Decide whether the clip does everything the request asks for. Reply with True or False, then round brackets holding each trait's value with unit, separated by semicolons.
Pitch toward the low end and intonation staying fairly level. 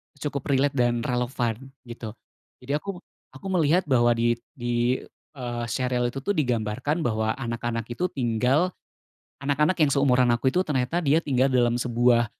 False (125 Hz; 3.2 semitones)